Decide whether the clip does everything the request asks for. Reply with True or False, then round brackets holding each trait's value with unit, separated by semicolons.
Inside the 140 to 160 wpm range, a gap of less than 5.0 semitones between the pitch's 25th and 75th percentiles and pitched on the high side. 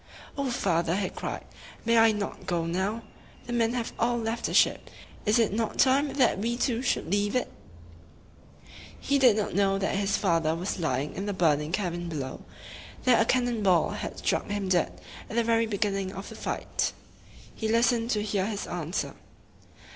False (190 wpm; 4.0 semitones; 205 Hz)